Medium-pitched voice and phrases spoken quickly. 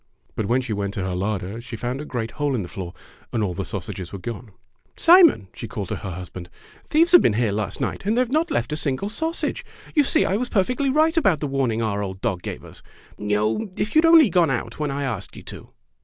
No: low, 125 Hz; fast, 250 wpm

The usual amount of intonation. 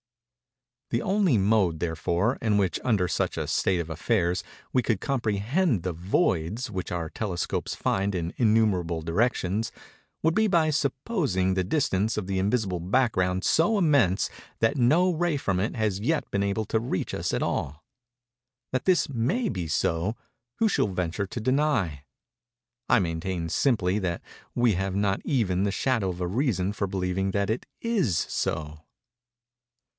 No: wide, 5.8 semitones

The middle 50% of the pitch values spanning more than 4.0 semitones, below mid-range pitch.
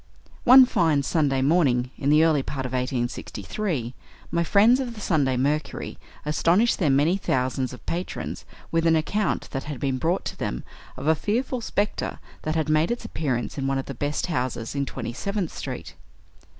No: average, 5.0 semitones; medium, 150 Hz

